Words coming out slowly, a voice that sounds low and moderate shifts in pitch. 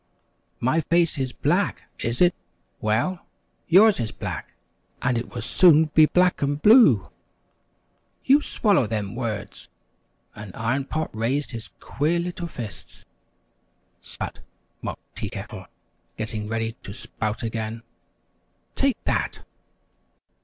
No: slow, 120 wpm; low, 130 Hz; wide, 7.3 semitones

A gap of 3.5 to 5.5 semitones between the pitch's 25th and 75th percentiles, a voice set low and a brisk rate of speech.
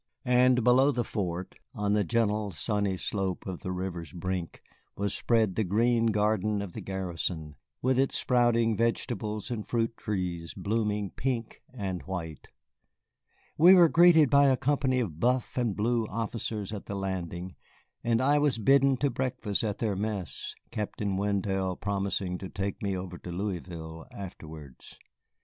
No: average, 4.2 semitones; low, 105 Hz; average, 155 wpm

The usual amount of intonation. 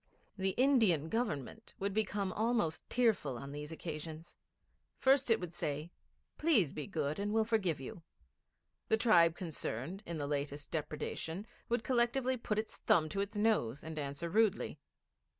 No: wide, 6.4 semitones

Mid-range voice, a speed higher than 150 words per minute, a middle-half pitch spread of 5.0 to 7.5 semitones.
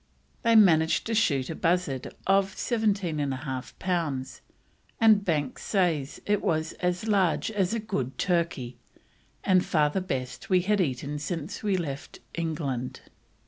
No: medium, 170 Hz; average, 140 wpm; average, 5.3 semitones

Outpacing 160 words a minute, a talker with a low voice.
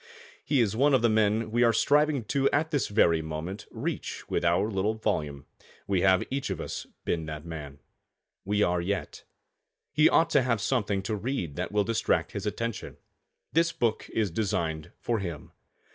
Yes: average, 175 wpm; low, 105 Hz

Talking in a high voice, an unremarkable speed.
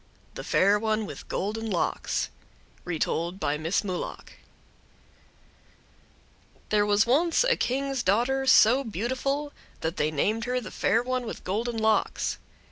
No: high, 225 Hz; slow, 130 wpm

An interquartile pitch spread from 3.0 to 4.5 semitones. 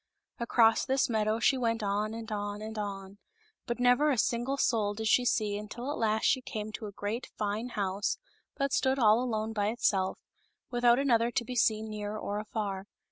No: narrow, 2.6 semitones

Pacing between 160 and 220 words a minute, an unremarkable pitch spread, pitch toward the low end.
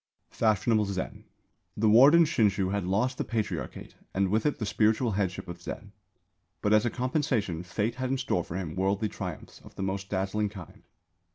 Yes: average, 180 wpm; average, 3.3 semitones; low, 105 Hz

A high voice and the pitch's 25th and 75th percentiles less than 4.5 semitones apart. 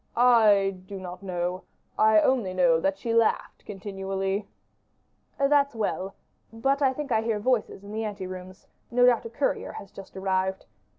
Yes: high, 205 Hz; average, 3.4 semitones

